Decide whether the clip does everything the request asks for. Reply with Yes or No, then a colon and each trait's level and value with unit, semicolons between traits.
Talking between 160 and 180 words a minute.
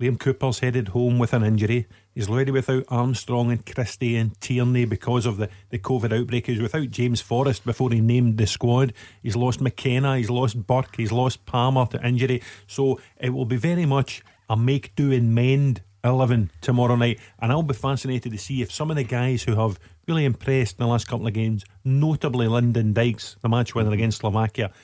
No: fast, 205 wpm